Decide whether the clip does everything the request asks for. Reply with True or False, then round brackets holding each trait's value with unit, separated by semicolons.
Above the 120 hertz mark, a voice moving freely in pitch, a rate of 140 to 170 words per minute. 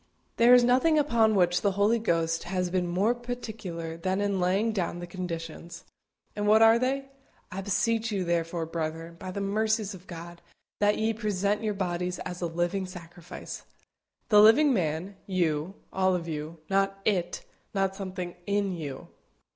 False (190 Hz; 3.6 semitones; 165 wpm)